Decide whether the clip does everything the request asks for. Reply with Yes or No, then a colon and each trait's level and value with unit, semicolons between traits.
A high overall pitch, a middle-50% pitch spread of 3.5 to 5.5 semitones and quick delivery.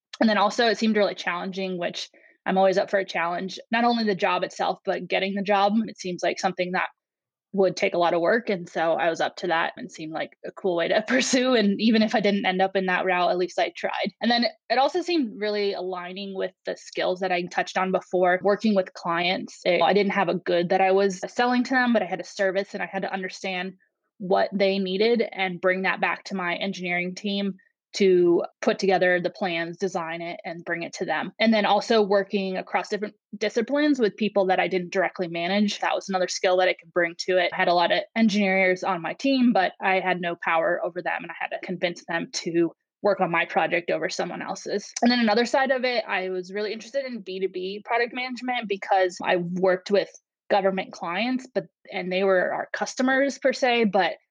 No: high, 195 Hz; average, 2.8 semitones; fast, 230 wpm